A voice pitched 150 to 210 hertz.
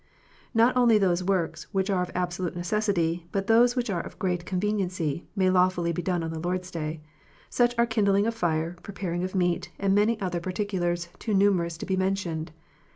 Yes: medium, 185 Hz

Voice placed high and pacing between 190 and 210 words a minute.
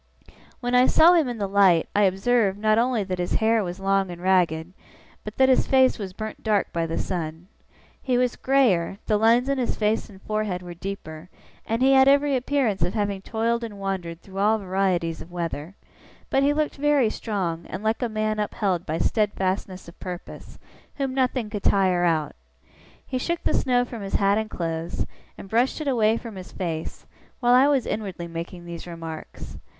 Yes: high, 205 Hz; average, 195 wpm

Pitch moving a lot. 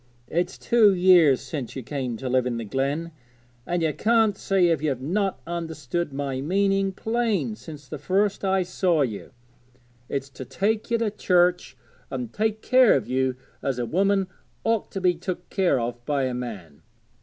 Yes: wide, 6.7 semitones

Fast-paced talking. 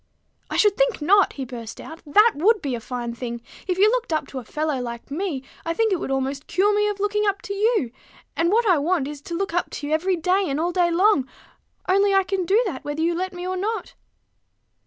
Yes: fast, 245 wpm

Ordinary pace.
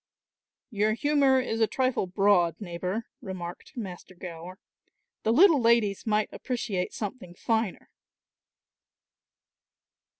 No: slow, 100 wpm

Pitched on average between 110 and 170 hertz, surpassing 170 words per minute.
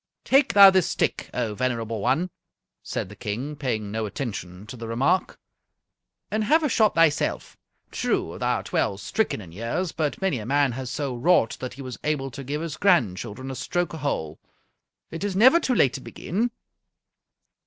Yes: low, 135 Hz; average, 185 wpm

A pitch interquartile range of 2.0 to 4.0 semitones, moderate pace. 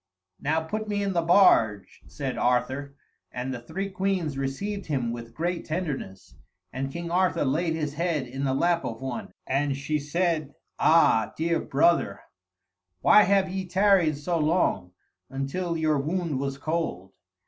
No: average, 4.6 semitones; average, 155 wpm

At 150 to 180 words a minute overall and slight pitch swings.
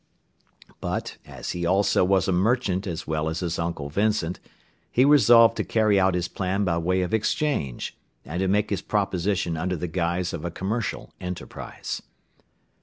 No: average, 170 wpm; average, 3.2 semitones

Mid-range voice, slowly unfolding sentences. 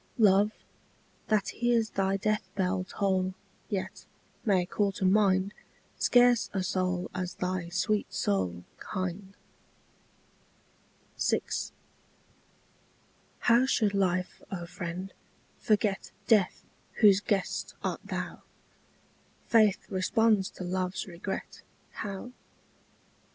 No: high, 195 Hz; slow, 100 wpm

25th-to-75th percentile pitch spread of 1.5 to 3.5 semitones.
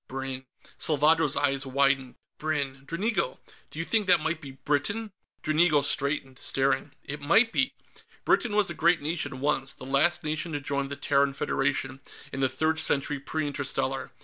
Yes: average, 2.9 semitones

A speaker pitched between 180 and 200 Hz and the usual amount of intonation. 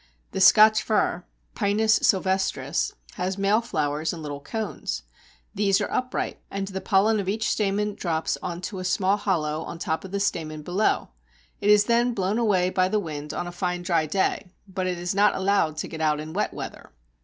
Yes: high, 190 Hz; average, 3.5 semitones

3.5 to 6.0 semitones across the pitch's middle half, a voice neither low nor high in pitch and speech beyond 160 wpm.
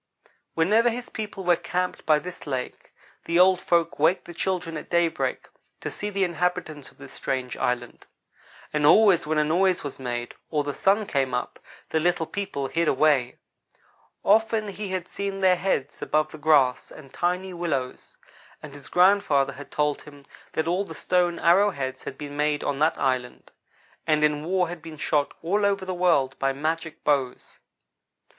Yes: average, 4.2 semitones; medium, 165 Hz; average, 180 wpm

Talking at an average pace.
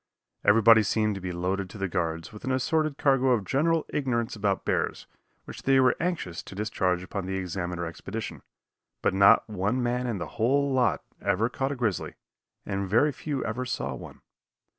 Yes: average, 185 wpm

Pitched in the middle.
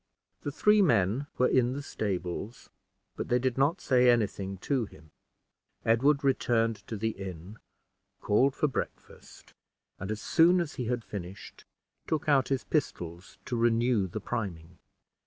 No: low, 115 Hz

